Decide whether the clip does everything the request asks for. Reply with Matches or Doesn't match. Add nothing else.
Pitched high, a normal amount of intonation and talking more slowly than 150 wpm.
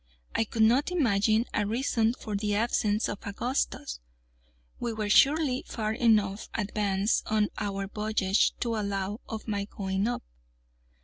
Doesn't match